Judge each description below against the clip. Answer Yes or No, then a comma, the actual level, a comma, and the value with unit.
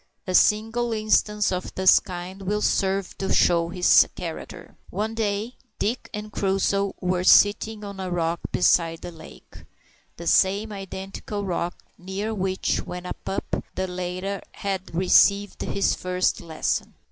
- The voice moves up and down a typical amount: No, narrow, 2.3 semitones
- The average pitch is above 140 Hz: Yes, high, 190 Hz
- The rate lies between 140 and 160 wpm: Yes, average, 145 wpm